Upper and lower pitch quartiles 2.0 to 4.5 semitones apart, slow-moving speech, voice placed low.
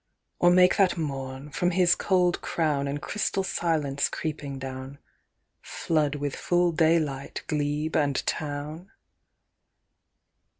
No: average, 3.6 semitones; slow, 115 wpm; medium, 150 Hz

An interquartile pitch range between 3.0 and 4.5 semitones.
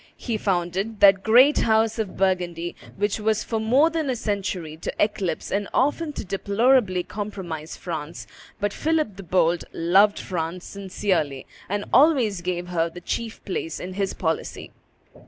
Yes: average, 3.9 semitones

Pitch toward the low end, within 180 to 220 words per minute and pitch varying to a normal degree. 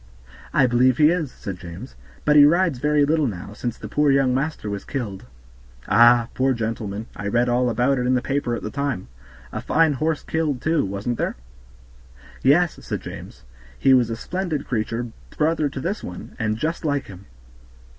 Yes: low, 130 Hz; average, 185 wpm; average, 4.8 semitones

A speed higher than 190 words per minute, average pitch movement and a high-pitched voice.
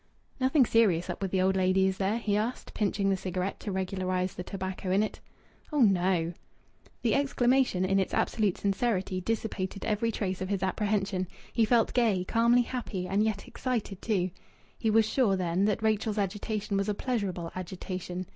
No: average, 175 wpm; average, 3.0 semitones; high, 195 Hz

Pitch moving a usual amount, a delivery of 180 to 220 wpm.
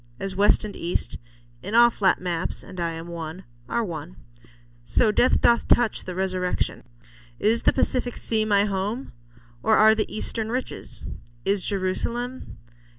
No: average, 3.8 semitones; average, 145 wpm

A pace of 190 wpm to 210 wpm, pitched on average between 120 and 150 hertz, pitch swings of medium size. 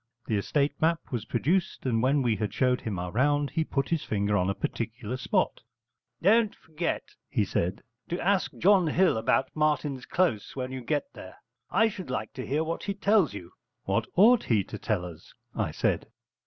No: average, 195 wpm; low, 135 Hz; wide, 7.3 semitones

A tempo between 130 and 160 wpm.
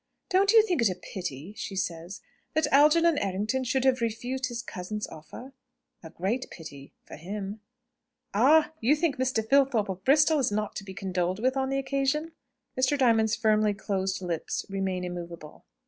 No: average, 170 wpm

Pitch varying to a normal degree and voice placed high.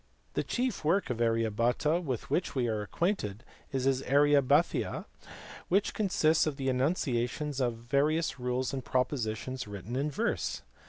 No: average, 4.1 semitones; low, 130 Hz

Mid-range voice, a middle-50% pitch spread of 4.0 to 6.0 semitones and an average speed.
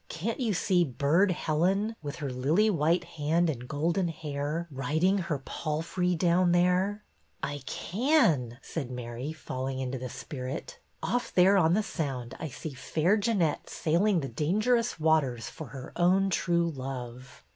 Yes: medium, 160 Hz; average, 5.0 semitones; average, 155 wpm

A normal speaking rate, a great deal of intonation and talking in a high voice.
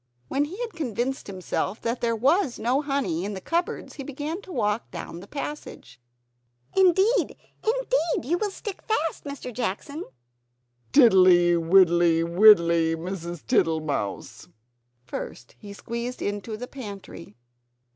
No: slow, 130 wpm; wide, 8.9 semitones; high, 230 Hz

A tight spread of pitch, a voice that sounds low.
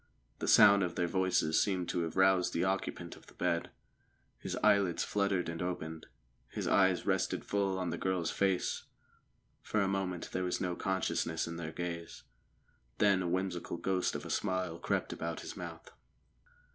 Yes: narrow, 2.0 semitones; very low, 90 Hz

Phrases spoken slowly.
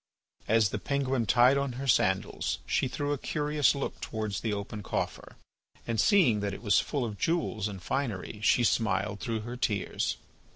No: average, 175 wpm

